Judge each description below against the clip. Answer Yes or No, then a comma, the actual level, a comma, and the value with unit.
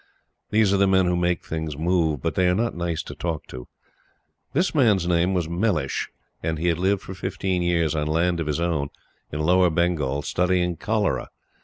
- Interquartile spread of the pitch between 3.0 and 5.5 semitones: No, narrow, 2.6 semitones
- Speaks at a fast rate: No, average, 195 wpm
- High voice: No, very low, 85 Hz